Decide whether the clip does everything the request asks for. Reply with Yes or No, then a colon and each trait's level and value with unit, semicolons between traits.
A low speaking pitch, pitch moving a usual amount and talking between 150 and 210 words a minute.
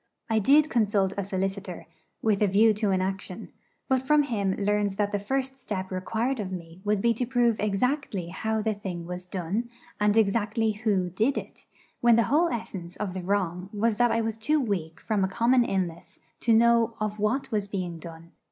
No: high, 210 Hz; average, 3.5 semitones; average, 200 wpm